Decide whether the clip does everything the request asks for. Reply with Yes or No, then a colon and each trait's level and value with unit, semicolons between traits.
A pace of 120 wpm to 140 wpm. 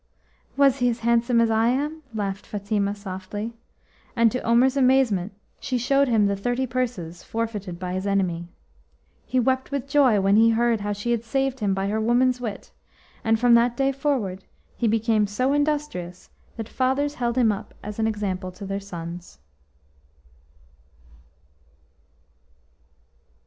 No: average, 155 wpm